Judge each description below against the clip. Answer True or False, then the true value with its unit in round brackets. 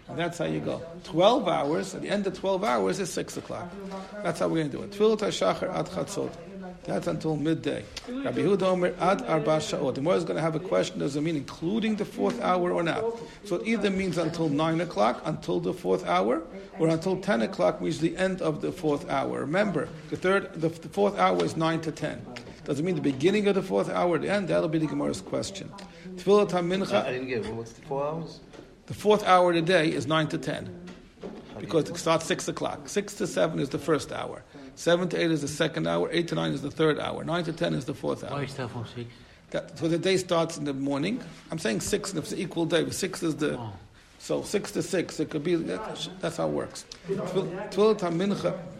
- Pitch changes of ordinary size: True (3.6 semitones)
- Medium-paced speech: False (215 wpm)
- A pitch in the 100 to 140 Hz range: False (170 Hz)